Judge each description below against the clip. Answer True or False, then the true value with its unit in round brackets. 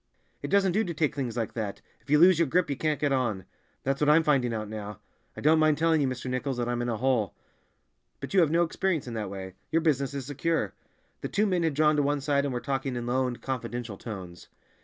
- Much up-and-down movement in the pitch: False (4.4 semitones)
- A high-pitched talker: False (135 Hz)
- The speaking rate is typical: False (255 wpm)